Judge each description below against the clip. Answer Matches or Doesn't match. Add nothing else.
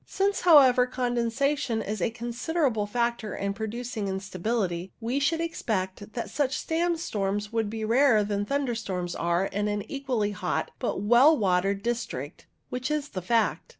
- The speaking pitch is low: Doesn't match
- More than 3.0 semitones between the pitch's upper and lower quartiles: Matches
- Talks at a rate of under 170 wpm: Matches